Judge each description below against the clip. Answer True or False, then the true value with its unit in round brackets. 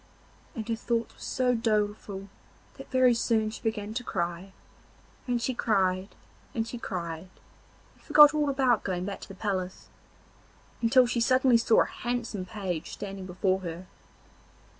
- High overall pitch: True (220 Hz)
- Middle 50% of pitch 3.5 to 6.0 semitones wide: True (4.2 semitones)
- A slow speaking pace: False (150 wpm)